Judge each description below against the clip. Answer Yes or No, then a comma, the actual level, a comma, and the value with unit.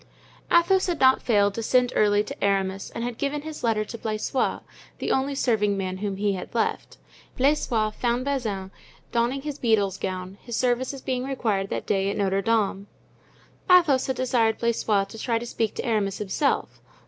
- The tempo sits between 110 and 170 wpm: No, average, 180 wpm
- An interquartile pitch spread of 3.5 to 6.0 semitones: Yes, average, 4.4 semitones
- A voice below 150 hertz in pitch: No, high, 225 Hz